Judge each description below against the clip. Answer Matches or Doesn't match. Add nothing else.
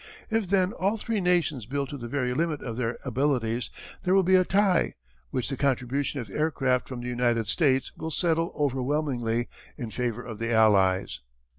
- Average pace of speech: Matches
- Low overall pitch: Matches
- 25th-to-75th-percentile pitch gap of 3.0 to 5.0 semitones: Doesn't match